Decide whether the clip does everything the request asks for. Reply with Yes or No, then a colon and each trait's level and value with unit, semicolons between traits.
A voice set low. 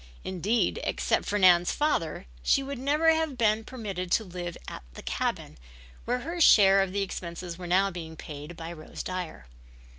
No: high, 190 Hz